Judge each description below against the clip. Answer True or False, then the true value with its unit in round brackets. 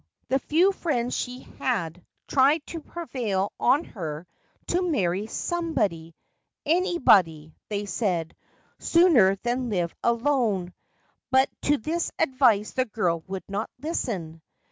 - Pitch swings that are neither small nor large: False (7.6 semitones)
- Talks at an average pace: False (125 wpm)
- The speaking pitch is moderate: False (235 Hz)